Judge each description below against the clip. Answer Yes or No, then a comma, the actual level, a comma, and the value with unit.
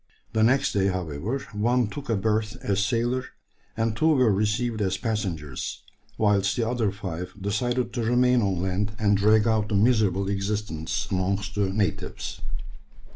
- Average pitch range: Yes, average, 3.0 semitones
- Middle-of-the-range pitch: No, low, 105 Hz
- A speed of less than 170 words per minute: Yes, average, 155 wpm